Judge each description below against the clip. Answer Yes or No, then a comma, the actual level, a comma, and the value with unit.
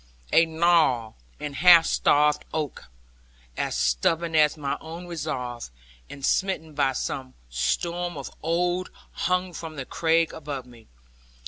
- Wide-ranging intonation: No, average, 3.8 semitones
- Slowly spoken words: Yes, slow, 130 wpm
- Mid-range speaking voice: Yes, medium, 155 Hz